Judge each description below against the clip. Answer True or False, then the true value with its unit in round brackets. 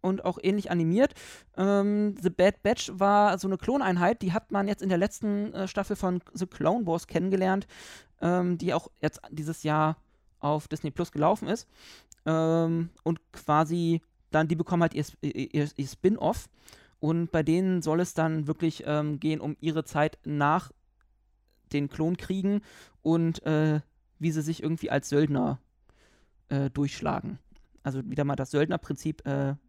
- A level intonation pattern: False (3.8 semitones)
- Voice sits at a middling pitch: True (160 Hz)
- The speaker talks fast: False (160 wpm)